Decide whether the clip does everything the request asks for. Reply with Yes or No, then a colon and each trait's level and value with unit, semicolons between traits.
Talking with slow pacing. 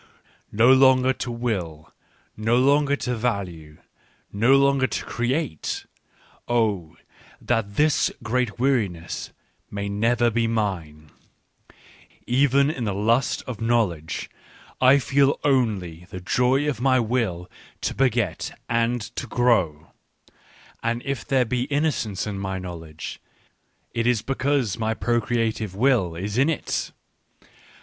Yes: slow, 125 wpm